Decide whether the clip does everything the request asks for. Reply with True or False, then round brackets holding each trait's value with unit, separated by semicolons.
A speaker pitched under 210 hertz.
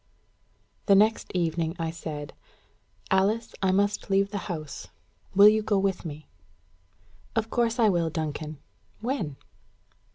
True (190 Hz)